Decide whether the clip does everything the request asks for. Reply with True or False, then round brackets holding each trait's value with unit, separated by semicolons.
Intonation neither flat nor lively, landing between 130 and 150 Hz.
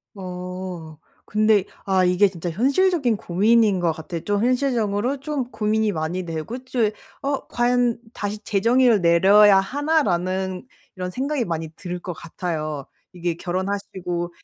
False (4.9 semitones; 195 Hz)